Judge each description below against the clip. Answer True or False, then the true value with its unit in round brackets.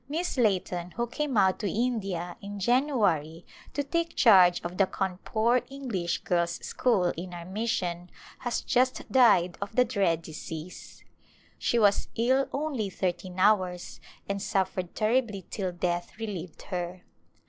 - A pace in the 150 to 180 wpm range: False (140 wpm)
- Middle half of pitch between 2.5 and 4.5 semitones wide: False (5.1 semitones)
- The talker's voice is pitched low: False (195 Hz)